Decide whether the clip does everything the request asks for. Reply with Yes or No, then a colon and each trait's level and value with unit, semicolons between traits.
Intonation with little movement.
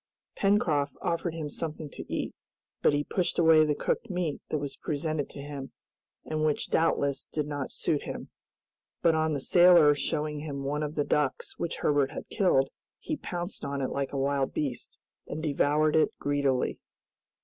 Yes: narrow, 2.2 semitones